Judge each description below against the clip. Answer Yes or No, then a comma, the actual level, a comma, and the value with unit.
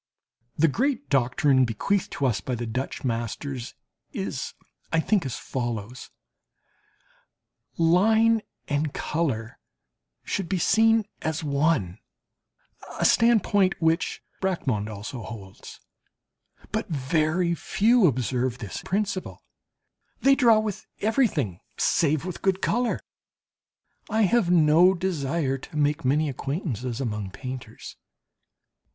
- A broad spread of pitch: Yes, wide, 7.1 semitones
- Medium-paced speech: No, slow, 110 wpm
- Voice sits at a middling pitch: Yes, medium, 150 Hz